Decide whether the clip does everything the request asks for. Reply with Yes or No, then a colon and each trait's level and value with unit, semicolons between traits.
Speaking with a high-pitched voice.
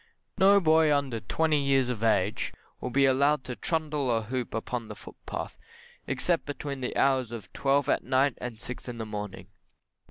No: low, 130 Hz